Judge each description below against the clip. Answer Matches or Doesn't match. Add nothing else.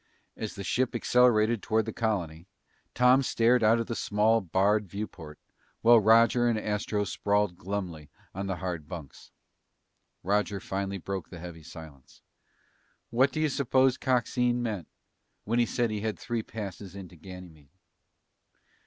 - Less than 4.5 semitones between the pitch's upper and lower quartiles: Matches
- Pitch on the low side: Matches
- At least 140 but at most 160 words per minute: Matches